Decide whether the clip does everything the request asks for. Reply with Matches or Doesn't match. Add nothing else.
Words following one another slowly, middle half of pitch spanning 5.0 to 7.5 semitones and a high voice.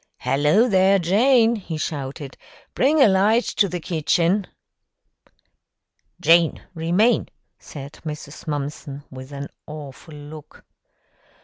Doesn't match